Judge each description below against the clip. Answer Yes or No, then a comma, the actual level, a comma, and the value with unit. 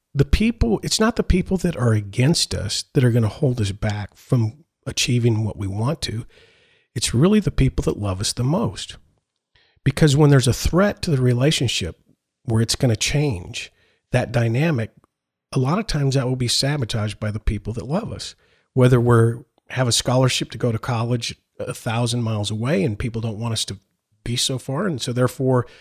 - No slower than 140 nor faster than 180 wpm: No, average, 200 wpm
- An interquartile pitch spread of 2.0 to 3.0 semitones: No, average, 4.0 semitones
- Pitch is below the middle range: Yes, low, 125 Hz